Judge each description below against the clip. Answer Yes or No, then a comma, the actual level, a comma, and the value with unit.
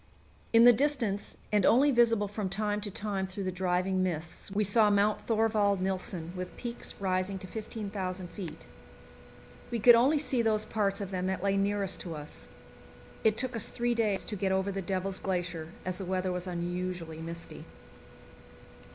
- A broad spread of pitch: No, average, 2.7 semitones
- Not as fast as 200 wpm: Yes, average, 175 wpm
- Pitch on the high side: Yes, high, 195 Hz